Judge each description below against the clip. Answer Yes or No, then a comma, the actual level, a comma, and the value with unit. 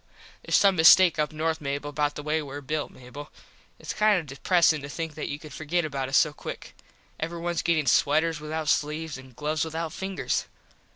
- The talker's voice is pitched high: No, medium, 155 Hz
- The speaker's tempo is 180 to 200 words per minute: Yes, average, 190 wpm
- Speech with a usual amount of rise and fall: No, narrow, 2.0 semitones